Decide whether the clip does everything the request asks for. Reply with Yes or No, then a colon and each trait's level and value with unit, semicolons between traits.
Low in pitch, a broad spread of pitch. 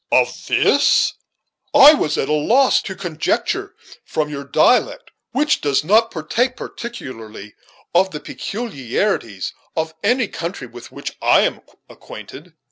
No: medium, 165 Hz; wide, 8.8 semitones